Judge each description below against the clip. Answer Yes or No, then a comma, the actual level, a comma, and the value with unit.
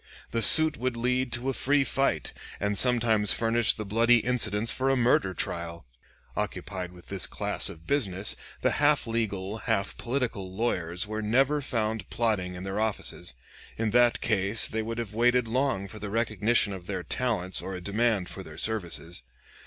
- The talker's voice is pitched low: Yes, low, 110 Hz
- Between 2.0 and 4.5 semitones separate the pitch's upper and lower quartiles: Yes, average, 3.9 semitones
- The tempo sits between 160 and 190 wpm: Yes, average, 175 wpm